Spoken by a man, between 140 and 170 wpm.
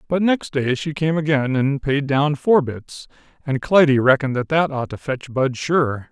No: male; fast, 205 wpm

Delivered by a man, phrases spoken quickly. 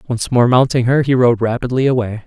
Yes: male; fast, 210 wpm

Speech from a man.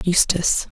No: female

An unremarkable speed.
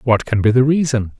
No: fast, 250 wpm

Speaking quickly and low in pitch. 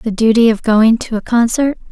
No: fast, 220 wpm; high, 225 Hz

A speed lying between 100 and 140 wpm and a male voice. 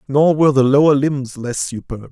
No: average, 200 wpm; male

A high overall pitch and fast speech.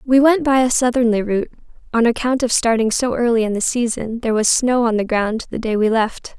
Yes: high, 235 Hz; fast, 235 wpm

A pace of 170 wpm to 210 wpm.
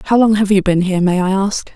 No: fast, 310 wpm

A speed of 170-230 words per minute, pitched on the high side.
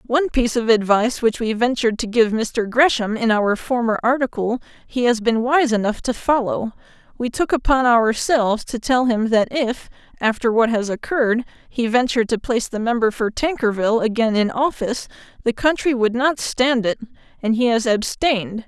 Yes: average, 175 wpm; high, 235 Hz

